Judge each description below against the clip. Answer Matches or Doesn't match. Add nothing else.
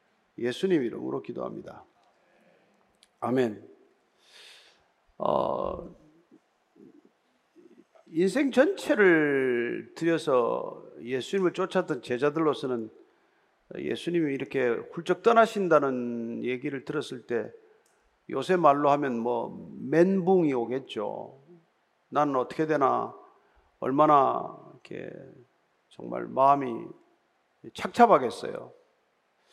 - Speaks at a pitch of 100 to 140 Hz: Doesn't match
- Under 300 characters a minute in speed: Matches